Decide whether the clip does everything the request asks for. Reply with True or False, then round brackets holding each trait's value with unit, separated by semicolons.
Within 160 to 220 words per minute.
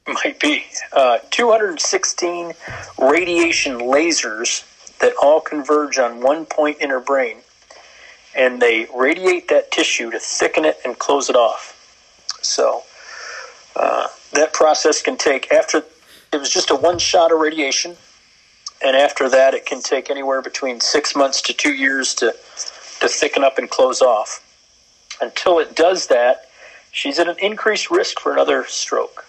False (150 wpm)